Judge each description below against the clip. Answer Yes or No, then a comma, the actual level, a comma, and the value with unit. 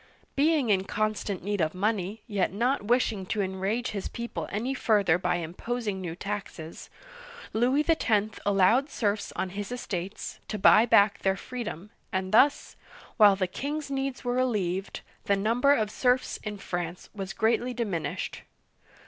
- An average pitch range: Yes, average, 4.3 semitones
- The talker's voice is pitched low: No, high, 210 Hz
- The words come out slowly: No, average, 150 wpm